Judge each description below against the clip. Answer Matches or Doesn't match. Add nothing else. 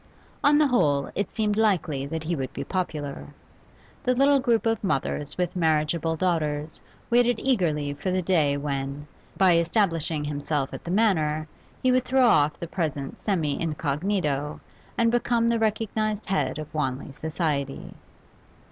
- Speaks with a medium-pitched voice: Matches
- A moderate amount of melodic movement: Doesn't match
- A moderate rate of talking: Matches